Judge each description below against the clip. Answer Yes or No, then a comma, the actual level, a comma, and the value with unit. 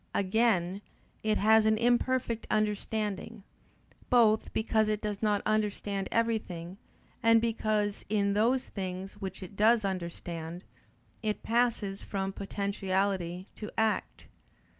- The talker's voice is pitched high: Yes, high, 210 Hz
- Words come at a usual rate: No, slow, 115 wpm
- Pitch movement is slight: Yes, narrow, 2.3 semitones